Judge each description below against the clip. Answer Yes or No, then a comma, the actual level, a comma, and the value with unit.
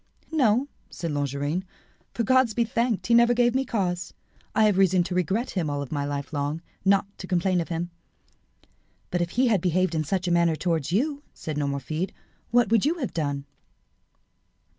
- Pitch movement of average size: No, wide, 6.4 semitones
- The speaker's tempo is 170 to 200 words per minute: Yes, average, 185 wpm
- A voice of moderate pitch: Yes, medium, 180 Hz